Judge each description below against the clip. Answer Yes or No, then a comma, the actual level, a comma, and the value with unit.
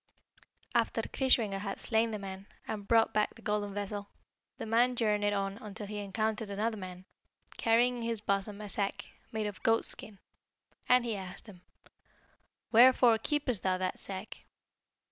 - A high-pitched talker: Yes, high, 210 Hz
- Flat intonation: Yes, narrow, 2.3 semitones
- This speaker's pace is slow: No, average, 155 wpm